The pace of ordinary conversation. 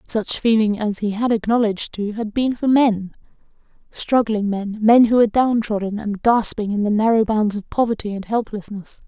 Yes: average, 180 wpm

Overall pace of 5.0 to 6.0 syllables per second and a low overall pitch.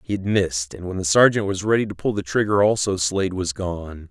Yes: 5.7 syllables/s; very low, 95 Hz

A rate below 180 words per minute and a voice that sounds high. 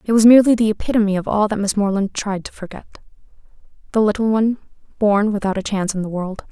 No: fast, 205 wpm; high, 205 Hz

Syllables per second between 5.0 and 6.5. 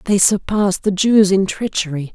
No: 4.5 syllables/s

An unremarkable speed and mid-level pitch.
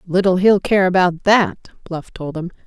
Yes: average, 180 wpm; medium, 180 Hz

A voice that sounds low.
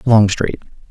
Yes: low, 110 Hz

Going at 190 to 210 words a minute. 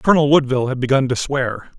Yes: average, 200 wpm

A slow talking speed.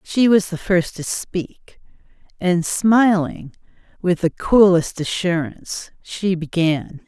Yes: slow, 120 wpm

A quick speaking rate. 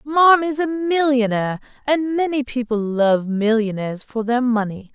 No: slow, 135 wpm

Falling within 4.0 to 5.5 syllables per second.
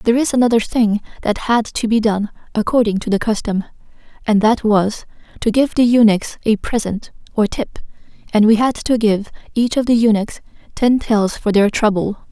Yes: 5.0 syllables/s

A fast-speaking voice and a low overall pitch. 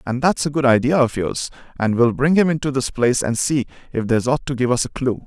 Yes: fast, 275 wpm; low, 130 Hz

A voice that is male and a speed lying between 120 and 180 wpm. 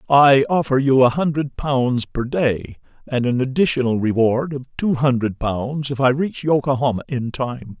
Yes: male; average, 170 wpm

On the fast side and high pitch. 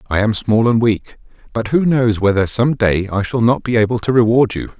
No: fast, 240 wpm; low, 115 Hz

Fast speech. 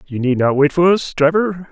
Yes: fast, 245 wpm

